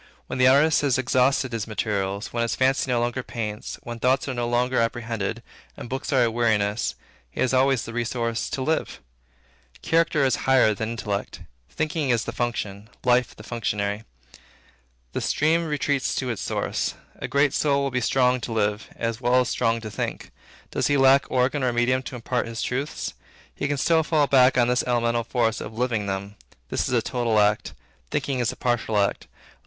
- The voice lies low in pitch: Yes, low, 120 Hz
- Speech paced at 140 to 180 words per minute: No, average, 195 wpm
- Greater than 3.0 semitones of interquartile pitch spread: No, narrow, 2.6 semitones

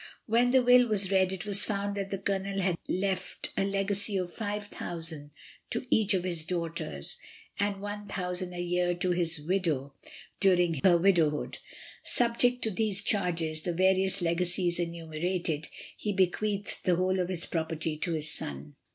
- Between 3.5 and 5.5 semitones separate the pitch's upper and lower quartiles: No, average, 2.9 semitones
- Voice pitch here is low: No, medium, 185 Hz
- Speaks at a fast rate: No, average, 160 wpm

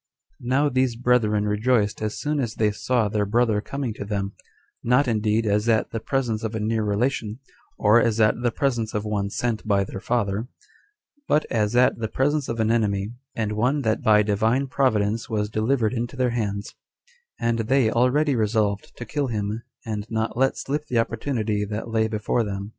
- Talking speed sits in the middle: Yes, average, 190 wpm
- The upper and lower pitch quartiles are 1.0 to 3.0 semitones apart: Yes, average, 2.7 semitones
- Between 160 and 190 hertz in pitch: No, low, 110 Hz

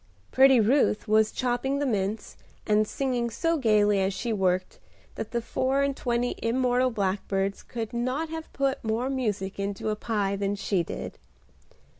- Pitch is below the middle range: No, high, 230 Hz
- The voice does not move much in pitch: No, average, 4.2 semitones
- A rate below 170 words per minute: Yes, average, 160 wpm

